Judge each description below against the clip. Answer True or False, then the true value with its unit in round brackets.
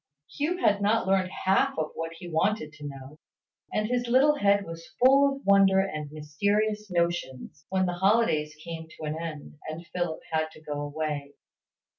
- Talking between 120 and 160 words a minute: False (170 wpm)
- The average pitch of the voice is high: False (175 Hz)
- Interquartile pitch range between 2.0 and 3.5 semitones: False (5.0 semitones)